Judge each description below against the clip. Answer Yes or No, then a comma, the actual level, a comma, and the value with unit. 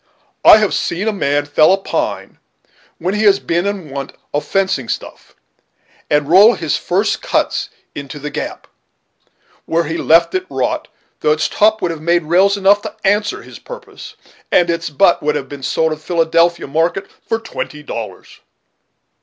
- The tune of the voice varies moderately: Yes, average, 4.5 semitones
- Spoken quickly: No, average, 175 wpm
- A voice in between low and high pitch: Yes, medium, 170 Hz